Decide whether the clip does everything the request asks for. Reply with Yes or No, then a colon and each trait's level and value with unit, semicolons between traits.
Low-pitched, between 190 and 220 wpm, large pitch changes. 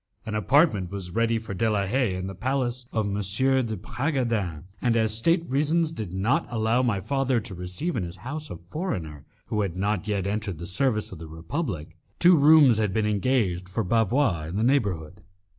Yes: low, 110 Hz; average, 200 wpm; wide, 5.8 semitones